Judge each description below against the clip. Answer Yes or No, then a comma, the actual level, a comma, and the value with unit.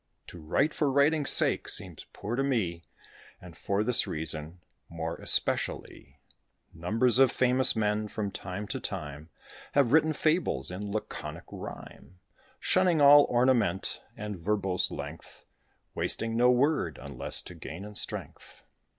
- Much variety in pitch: Yes, wide, 6.9 semitones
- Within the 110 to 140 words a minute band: Yes, slow, 135 wpm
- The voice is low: Yes, low, 105 Hz